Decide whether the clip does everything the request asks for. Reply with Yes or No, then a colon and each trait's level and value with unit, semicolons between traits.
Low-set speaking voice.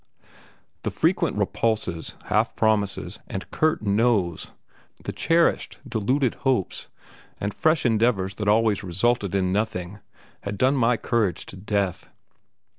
Yes: low, 105 Hz